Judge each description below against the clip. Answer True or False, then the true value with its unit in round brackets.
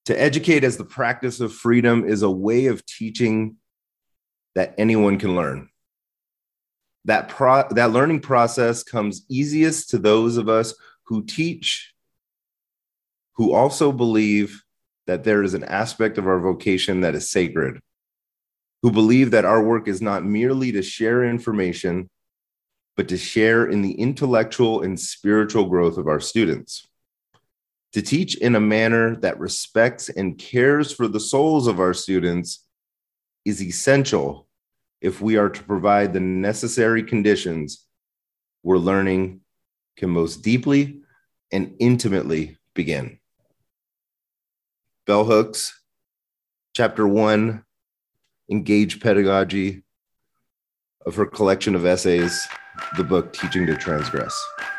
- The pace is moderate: False (125 wpm)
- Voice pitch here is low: True (110 Hz)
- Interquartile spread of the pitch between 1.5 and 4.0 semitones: True (3.7 semitones)